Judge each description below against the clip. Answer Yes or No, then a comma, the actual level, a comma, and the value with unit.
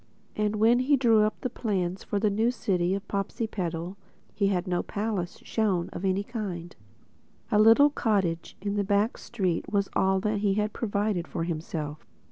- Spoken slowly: No, average, 175 wpm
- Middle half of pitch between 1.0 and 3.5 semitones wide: Yes, average, 3.0 semitones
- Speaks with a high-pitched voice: Yes, high, 200 Hz